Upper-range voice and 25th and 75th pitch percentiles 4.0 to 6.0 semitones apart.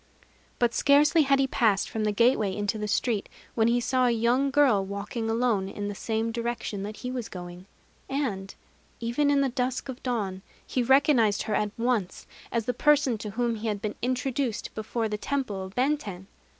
No: high, 230 Hz; average, 3.6 semitones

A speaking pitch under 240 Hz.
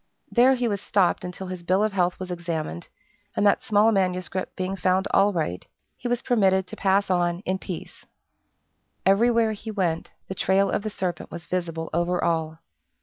Yes: medium, 185 Hz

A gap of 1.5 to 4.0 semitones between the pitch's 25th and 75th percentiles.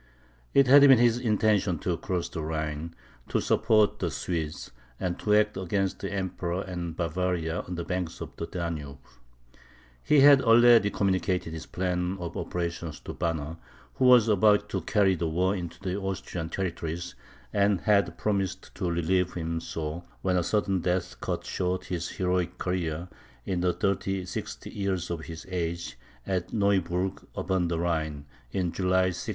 Yes: narrow, 2.6 semitones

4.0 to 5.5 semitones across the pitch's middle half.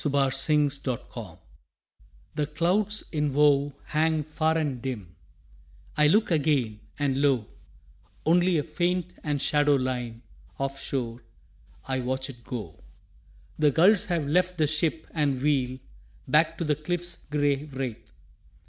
No: average, 3.2 semitones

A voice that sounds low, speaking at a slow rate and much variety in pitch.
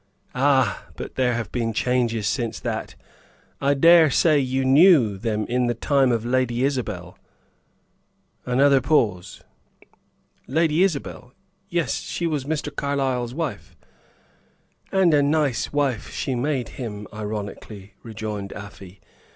No: low, 125 Hz; slow, 125 wpm; average, 4.2 semitones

